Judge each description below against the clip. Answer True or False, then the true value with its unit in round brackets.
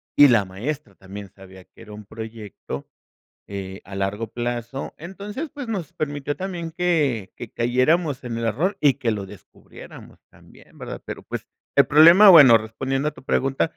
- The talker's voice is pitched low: True (130 Hz)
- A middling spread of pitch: False (6.8 semitones)